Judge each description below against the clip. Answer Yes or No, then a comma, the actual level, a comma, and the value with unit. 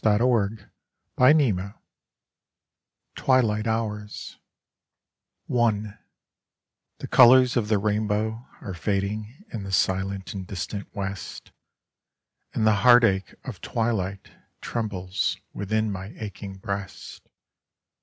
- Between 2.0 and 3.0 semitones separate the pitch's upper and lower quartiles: Yes, narrow, 2.5 semitones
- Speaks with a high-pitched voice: No, low, 105 Hz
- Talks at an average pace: No, slow, 95 wpm